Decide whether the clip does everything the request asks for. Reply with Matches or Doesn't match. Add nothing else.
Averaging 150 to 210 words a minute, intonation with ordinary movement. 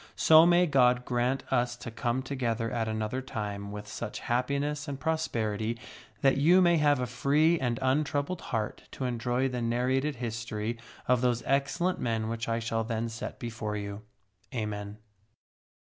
Matches